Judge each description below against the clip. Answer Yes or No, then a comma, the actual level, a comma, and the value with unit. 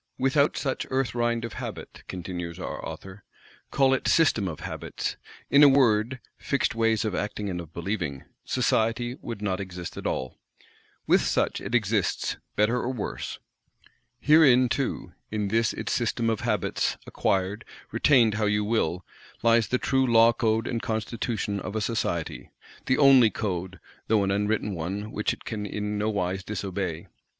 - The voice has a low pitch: Yes, low, 110 Hz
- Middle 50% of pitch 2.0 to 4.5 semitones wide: Yes, average, 3.5 semitones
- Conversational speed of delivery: Yes, average, 160 wpm